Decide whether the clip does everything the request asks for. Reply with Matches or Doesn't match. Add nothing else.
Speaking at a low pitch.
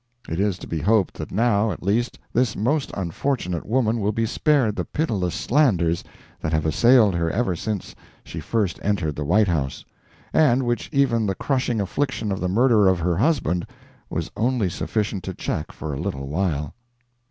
Matches